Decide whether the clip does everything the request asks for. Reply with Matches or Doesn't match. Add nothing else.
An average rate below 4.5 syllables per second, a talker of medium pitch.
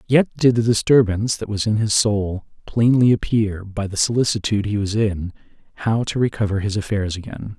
Doesn't match